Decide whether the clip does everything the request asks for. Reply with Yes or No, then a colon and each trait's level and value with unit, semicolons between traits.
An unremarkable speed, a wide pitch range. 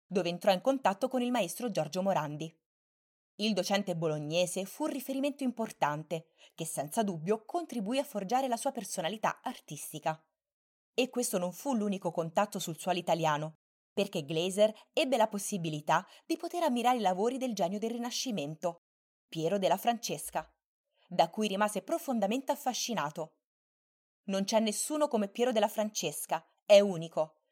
Yes: average, 145 wpm; wide, 6.3 semitones